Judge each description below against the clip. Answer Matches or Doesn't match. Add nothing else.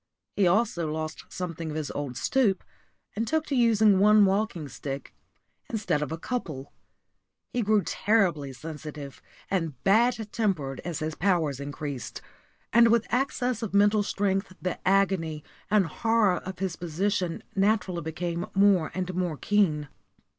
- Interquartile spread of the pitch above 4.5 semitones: Matches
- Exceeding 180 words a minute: Doesn't match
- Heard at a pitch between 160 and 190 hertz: Matches